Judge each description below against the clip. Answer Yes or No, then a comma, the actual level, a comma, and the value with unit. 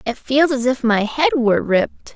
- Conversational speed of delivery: No, fast, 225 wpm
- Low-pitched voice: No, very high, 250 Hz